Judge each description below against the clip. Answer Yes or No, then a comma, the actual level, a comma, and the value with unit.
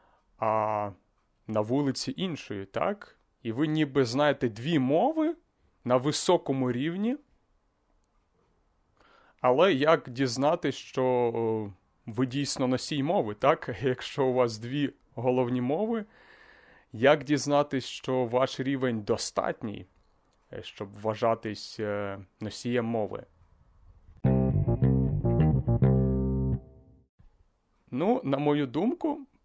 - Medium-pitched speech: No, low, 125 Hz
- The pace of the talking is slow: Yes, slow, 90 wpm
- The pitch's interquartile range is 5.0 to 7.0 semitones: Yes, wide, 5.4 semitones